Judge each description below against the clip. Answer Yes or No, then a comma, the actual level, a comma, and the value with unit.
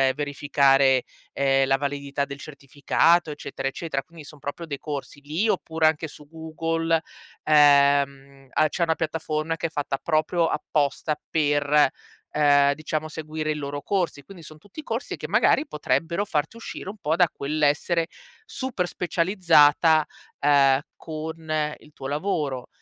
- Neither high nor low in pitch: Yes, medium, 150 Hz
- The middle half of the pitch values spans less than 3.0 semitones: Yes, narrow, 2.4 semitones